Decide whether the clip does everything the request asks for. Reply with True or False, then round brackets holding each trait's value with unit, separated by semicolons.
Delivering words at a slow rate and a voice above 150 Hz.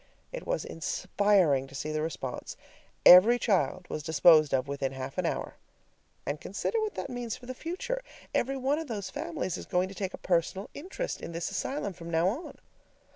False (190 wpm; 190 Hz)